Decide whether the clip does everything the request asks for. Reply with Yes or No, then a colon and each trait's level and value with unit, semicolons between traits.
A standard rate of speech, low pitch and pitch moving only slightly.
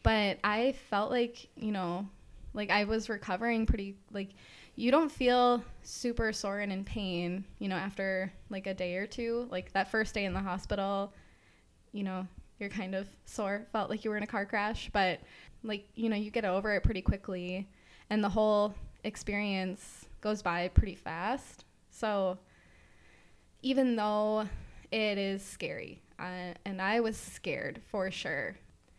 No: average, 165 wpm; high, 205 Hz; narrow, 2.3 semitones